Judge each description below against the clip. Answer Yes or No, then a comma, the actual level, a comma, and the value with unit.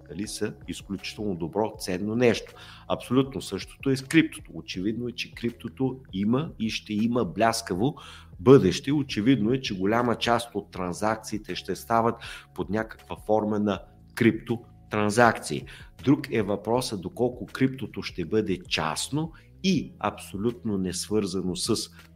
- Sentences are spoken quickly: No, average, 130 wpm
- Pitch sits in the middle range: No, low, 105 Hz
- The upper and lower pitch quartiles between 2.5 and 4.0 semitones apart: No, average, 4.5 semitones